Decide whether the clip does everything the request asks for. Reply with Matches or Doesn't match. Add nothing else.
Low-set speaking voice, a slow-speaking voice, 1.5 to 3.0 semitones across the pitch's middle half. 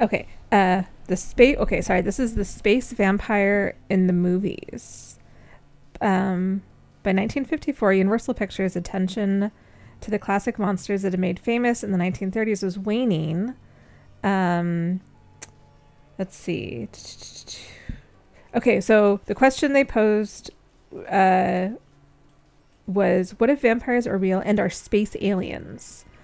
Doesn't match